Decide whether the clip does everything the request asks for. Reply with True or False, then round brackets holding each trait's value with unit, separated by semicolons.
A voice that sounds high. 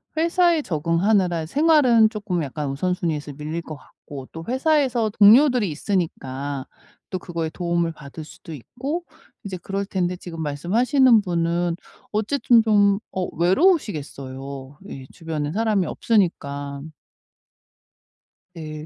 False (175 Hz)